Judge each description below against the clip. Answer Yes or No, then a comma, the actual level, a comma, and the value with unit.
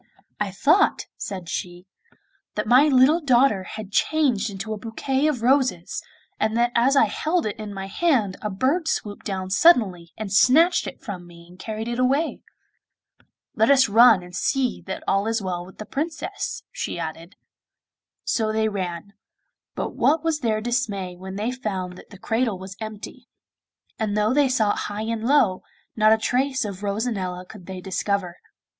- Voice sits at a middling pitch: No, high, 215 Hz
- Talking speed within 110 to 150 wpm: No, average, 175 wpm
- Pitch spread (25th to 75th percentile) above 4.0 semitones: Yes, average, 5.0 semitones